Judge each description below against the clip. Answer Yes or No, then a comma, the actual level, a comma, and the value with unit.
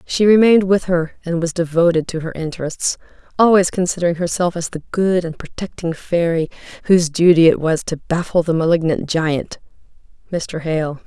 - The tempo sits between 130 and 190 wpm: Yes, average, 165 wpm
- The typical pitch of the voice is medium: Yes, medium, 170 Hz